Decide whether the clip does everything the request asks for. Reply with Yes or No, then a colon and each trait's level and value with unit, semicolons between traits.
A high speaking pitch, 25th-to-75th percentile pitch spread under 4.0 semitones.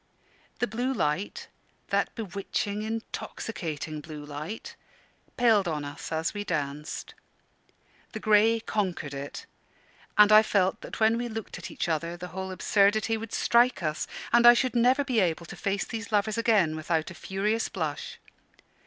No: high, 200 Hz; wide, 5.6 semitones